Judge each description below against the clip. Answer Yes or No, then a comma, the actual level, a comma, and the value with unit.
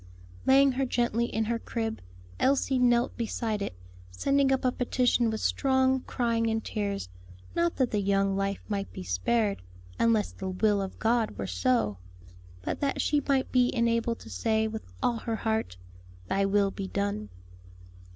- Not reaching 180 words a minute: Yes, average, 165 wpm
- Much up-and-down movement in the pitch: No, average, 3.6 semitones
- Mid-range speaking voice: No, high, 220 Hz